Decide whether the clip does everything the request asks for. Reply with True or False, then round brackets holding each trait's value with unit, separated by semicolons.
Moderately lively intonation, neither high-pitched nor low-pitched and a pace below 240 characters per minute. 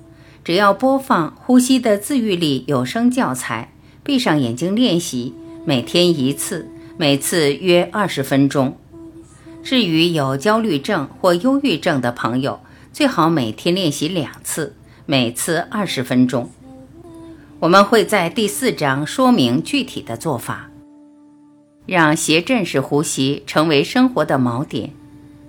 False (7.6 semitones; 160 Hz; 200 characters per minute)